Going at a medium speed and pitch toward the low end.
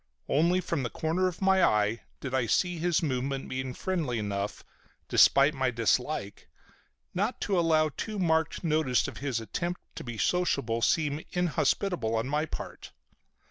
No: average, 155 wpm; medium, 150 Hz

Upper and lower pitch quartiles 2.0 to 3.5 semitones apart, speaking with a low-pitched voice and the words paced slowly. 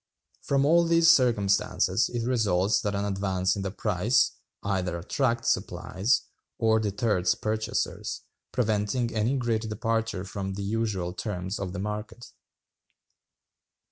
Yes: average, 3.2 semitones; low, 105 Hz; slow, 125 wpm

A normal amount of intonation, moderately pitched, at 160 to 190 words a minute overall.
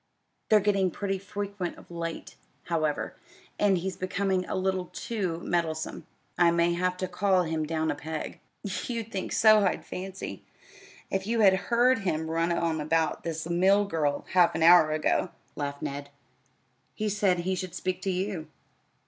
Yes: average, 3.0 semitones; medium, 180 Hz; average, 165 wpm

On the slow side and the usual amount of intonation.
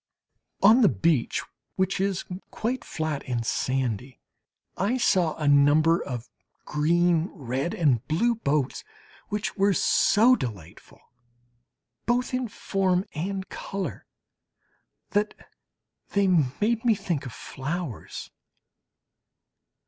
No: slow, 105 wpm; wide, 6.4 semitones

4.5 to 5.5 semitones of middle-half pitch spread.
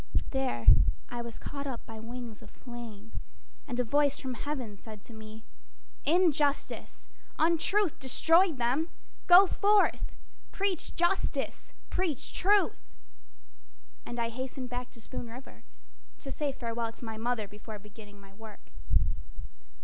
Yes: average, 5.0 semitones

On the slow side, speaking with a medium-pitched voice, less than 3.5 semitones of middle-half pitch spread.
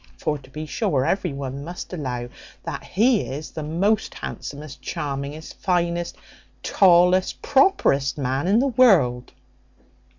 No: slow, 130 wpm; medium, 155 Hz; average, 5.2 semitones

